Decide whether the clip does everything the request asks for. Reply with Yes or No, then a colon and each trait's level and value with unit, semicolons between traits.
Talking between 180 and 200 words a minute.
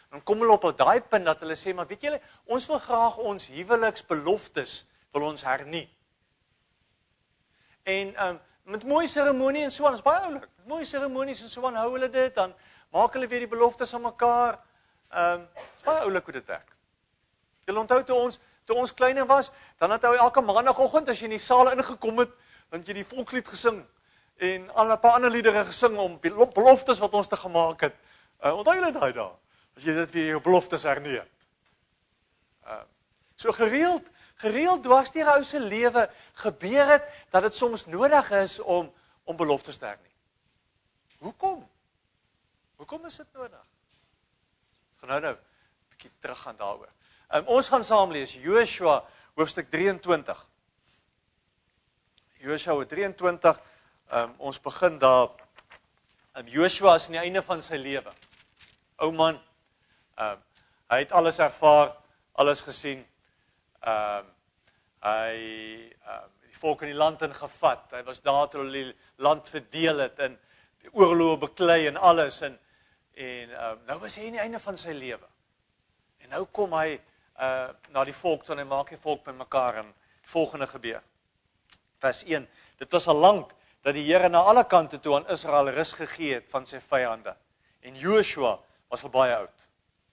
No: average, 170 wpm